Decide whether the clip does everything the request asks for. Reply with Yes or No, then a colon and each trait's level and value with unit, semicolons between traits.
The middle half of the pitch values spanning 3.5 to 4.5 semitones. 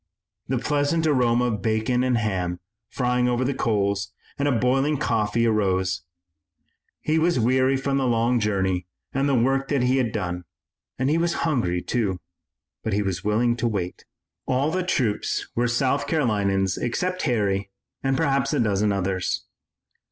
No: average, 4.9 semitones